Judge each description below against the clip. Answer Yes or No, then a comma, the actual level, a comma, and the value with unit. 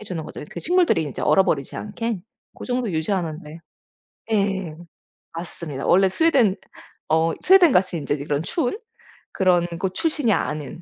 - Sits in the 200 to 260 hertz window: No, medium, 185 Hz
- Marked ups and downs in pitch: Yes, wide, 6.1 semitones